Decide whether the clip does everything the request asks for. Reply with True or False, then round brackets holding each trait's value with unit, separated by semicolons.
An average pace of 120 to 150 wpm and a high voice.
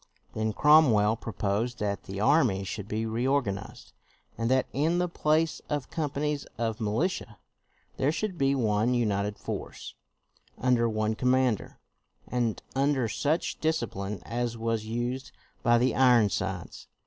False (135 wpm; 120 Hz)